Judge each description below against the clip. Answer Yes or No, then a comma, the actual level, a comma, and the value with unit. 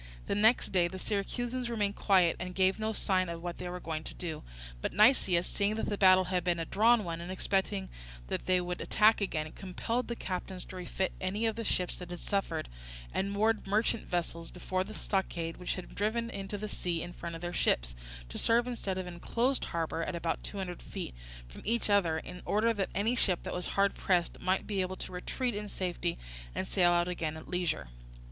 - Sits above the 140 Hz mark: Yes, medium, 185 Hz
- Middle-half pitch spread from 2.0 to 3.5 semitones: Yes, average, 3.1 semitones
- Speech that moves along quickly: Yes, fast, 220 wpm